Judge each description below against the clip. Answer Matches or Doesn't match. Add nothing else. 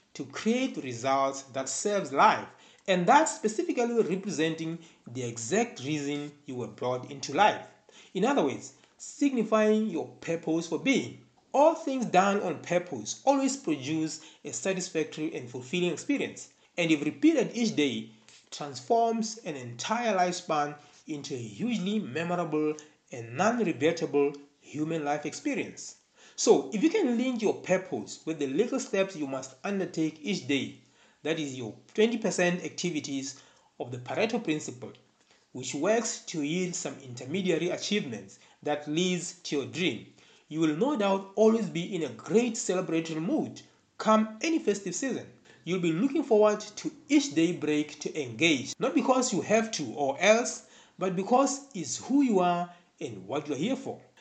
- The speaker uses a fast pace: Doesn't match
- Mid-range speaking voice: Matches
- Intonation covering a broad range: Matches